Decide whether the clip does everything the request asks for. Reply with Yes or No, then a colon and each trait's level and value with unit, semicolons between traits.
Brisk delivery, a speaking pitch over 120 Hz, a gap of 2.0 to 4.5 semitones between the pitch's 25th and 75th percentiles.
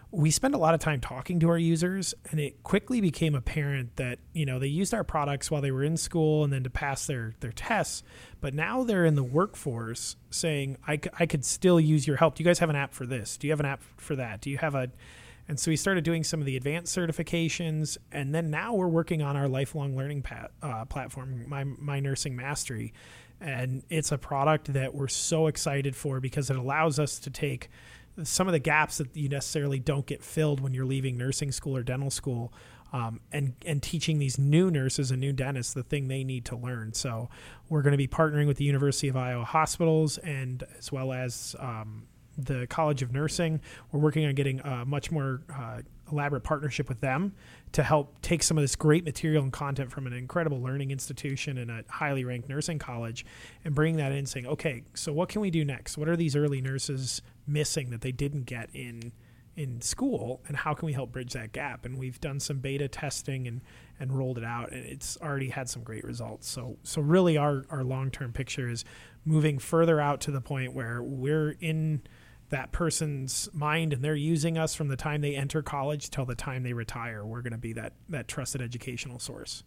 Yes: fast, 220 wpm; medium, 140 Hz; average, 3.1 semitones